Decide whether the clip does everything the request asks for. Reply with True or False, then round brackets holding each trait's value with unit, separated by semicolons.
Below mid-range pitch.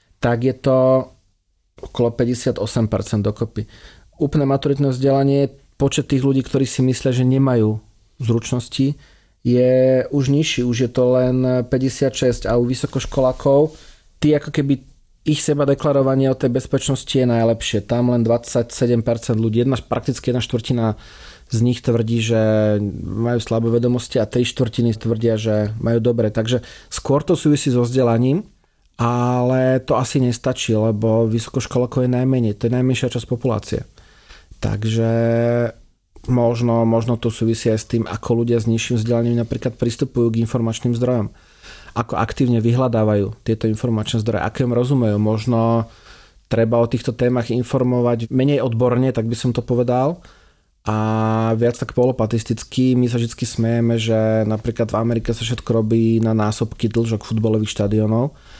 True (120 Hz)